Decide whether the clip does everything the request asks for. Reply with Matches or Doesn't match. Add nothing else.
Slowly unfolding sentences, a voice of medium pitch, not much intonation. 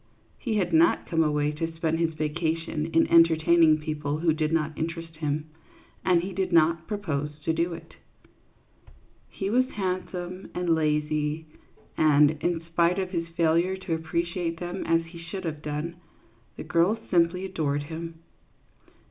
Doesn't match